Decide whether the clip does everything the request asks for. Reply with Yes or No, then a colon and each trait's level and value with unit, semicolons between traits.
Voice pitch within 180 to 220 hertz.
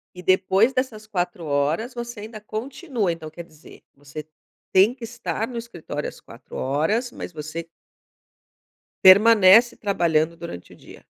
Yes: high, 190 Hz